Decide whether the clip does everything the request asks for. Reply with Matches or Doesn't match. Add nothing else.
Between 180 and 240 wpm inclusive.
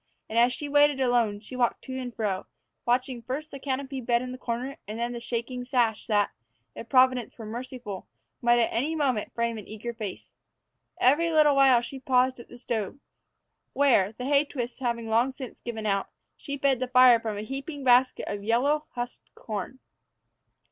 Matches